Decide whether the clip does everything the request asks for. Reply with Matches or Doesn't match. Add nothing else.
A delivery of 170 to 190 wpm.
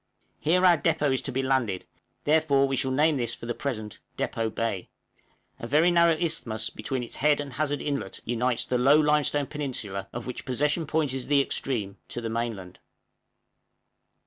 Matches